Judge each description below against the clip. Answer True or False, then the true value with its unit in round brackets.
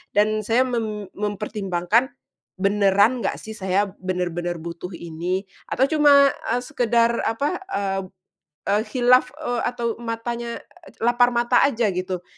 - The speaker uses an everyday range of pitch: True (4.1 semitones)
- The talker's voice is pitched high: True (215 Hz)